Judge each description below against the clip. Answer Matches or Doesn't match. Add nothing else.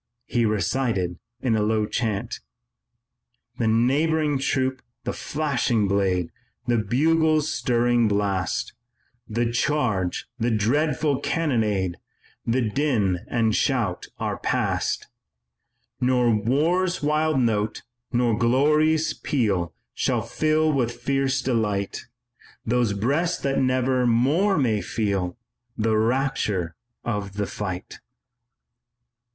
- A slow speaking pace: Matches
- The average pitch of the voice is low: Matches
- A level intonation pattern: Doesn't match